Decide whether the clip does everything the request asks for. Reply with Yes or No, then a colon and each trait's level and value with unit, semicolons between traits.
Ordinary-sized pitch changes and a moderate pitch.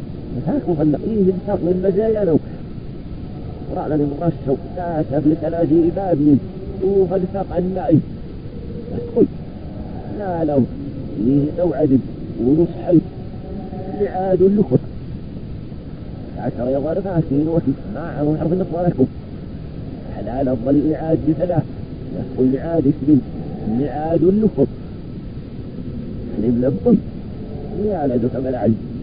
Yes: average, 4.9 semitones; medium, 155 Hz